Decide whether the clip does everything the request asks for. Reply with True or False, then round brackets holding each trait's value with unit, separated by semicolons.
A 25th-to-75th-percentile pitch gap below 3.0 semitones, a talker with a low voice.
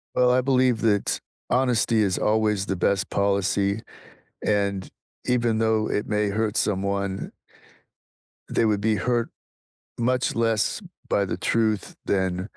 True (2.6 semitones; 105 Hz)